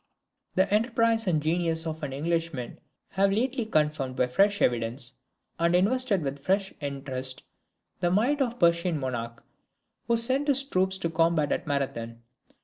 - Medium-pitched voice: Yes, medium, 170 Hz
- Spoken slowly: No, average, 150 wpm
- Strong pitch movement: Yes, wide, 6.6 semitones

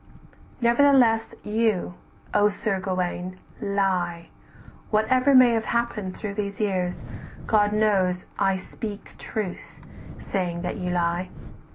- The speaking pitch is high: Yes, high, 200 Hz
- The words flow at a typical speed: No, slow, 110 wpm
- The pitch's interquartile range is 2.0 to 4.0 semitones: Yes, average, 3.2 semitones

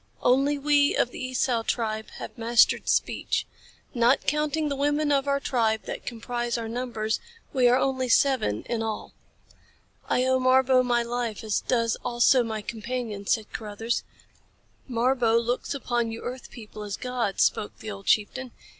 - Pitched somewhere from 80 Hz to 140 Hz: No, high, 240 Hz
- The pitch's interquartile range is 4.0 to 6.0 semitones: No, narrow, 2.6 semitones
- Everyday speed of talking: Yes, average, 160 wpm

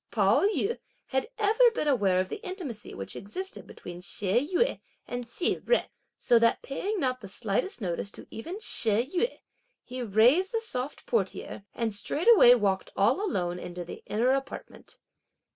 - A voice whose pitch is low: No, high, 245 Hz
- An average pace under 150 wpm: No, average, 160 wpm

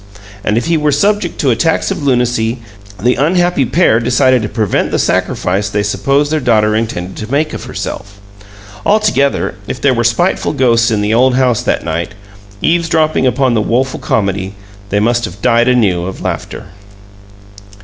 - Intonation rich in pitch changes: No, average, 4.8 semitones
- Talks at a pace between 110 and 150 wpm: No, average, 170 wpm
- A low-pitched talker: Yes, low, 120 Hz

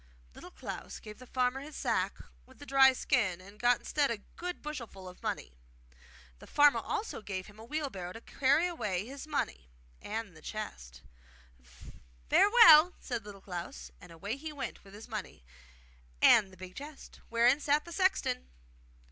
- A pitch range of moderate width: No, wide, 7.5 semitones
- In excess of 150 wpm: Yes, average, 165 wpm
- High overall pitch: Yes, high, 230 Hz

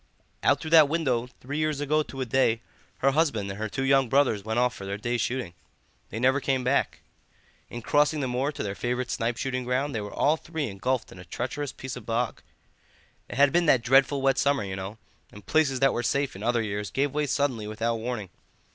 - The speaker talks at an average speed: No, fast, 225 wpm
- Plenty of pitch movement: No, average, 3.7 semitones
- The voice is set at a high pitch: No, low, 125 Hz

